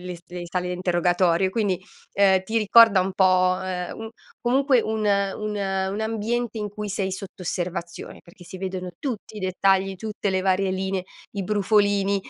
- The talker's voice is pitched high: Yes, high, 195 Hz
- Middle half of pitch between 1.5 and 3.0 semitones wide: Yes, narrow, 2.5 semitones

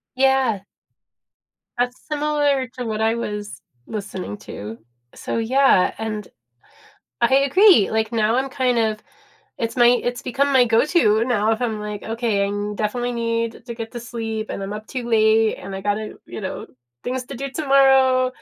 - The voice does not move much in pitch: No, average, 3.1 semitones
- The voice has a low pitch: No, high, 230 Hz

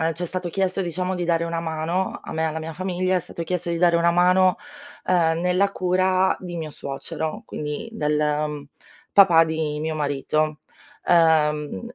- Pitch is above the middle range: No, medium, 170 Hz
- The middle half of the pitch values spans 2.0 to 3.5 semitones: Yes, average, 2.7 semitones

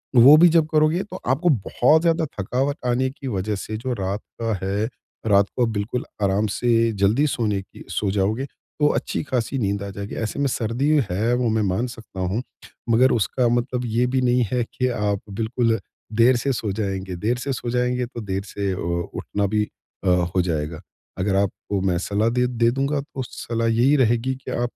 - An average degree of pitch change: Yes, average, 4.1 semitones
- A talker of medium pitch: No, low, 115 Hz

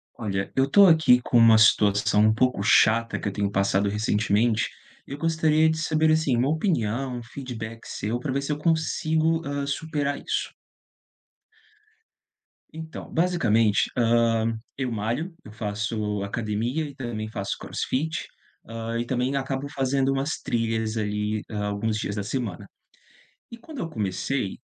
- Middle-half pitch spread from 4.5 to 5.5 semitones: Yes, average, 4.9 semitones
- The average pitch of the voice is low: Yes, low, 120 Hz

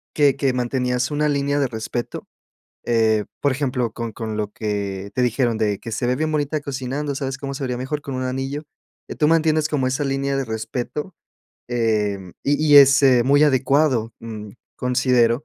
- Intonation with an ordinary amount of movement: Yes, average, 3.6 semitones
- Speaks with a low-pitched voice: Yes, low, 130 Hz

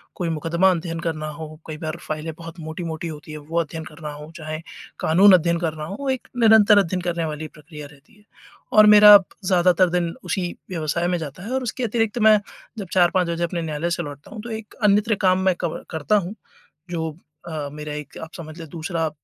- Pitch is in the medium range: Yes, medium, 170 Hz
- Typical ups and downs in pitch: Yes, average, 3.3 semitones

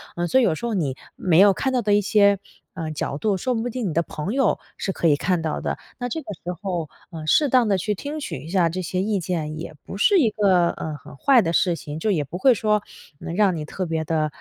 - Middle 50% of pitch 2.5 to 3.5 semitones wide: No, average, 4.8 semitones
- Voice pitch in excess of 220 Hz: No, medium, 185 Hz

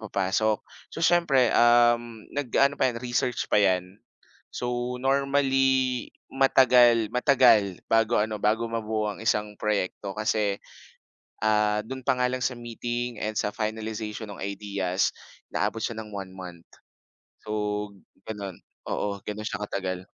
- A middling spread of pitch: Yes, average, 3.1 semitones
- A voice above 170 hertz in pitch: No, low, 110 Hz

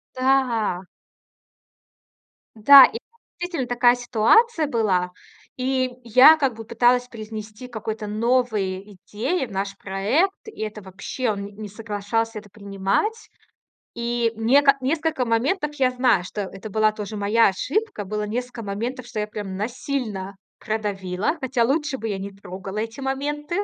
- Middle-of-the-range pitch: No, high, 225 Hz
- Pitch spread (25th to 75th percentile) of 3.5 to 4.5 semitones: Yes, average, 4.1 semitones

